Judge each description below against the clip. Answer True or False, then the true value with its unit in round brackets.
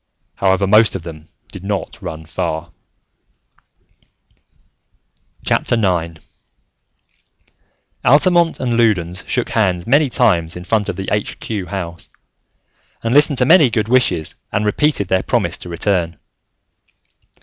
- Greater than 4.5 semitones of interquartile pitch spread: True (5.2 semitones)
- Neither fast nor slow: False (120 wpm)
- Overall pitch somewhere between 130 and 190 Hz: False (100 Hz)